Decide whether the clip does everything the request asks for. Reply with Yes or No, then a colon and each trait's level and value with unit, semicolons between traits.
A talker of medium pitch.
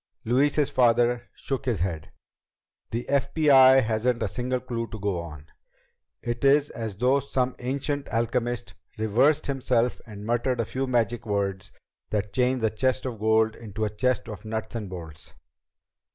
No: low, 120 Hz